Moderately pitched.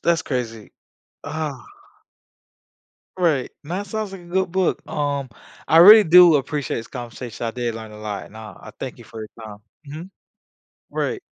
Yes: medium, 145 Hz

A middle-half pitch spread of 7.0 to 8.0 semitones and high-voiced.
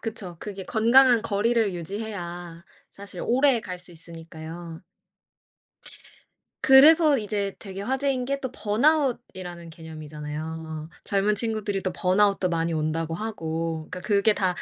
No: average, 5.2 semitones; high, 195 Hz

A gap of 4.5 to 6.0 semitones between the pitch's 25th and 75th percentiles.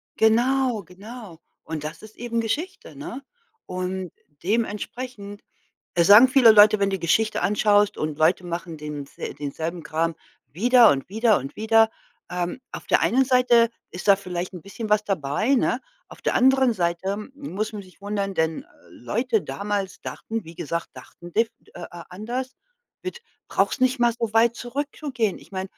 Yes: average, 5.2 semitones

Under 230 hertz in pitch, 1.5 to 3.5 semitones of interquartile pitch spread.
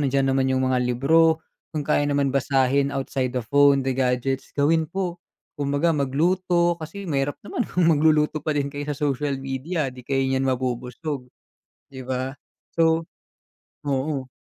Yes: medium, 140 Hz; average, 2.8 semitones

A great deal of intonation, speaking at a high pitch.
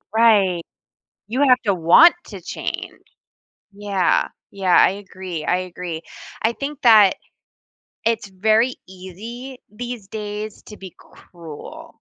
No: average, 3.8 semitones; high, 205 Hz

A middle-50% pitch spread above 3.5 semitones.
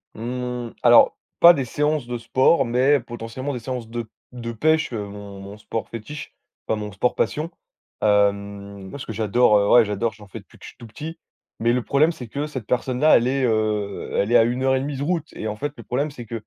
Yes: average, 4.0 semitones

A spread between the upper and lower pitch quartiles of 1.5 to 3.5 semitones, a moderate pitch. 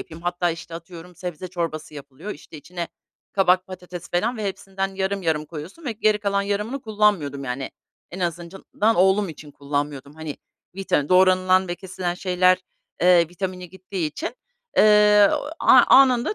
Yes: average, 3.1 semitones; medium, 180 Hz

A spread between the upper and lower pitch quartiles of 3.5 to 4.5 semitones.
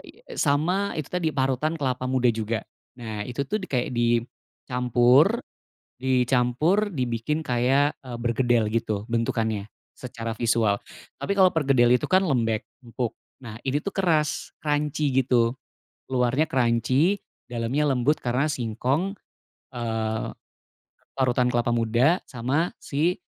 Yes: average, 4.2 semitones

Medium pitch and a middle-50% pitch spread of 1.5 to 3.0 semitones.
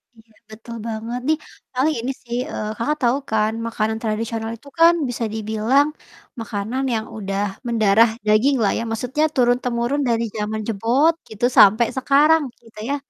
No: high, 230 Hz; average, 2.7 semitones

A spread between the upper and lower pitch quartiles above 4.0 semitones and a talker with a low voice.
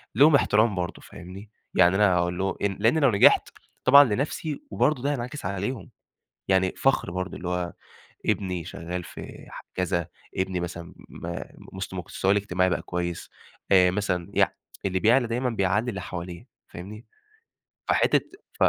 Yes: average, 4.5 semitones; very low, 95 Hz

